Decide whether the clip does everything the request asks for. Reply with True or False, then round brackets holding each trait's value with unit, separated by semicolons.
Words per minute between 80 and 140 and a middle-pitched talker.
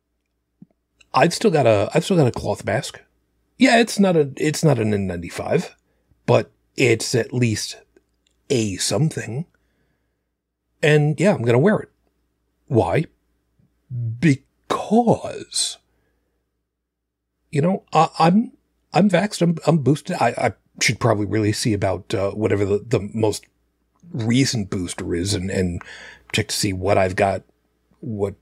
False (135 wpm; 105 Hz)